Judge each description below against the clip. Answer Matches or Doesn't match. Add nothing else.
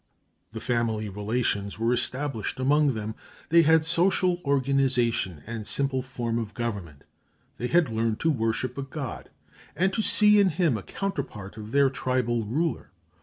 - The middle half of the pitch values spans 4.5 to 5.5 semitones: Matches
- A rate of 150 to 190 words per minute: Matches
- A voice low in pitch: Matches